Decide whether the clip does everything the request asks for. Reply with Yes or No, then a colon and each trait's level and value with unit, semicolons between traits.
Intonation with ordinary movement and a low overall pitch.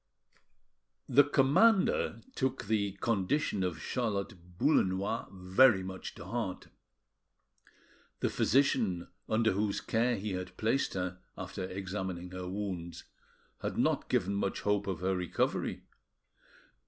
Yes: average, 4.1 semitones; low, 100 Hz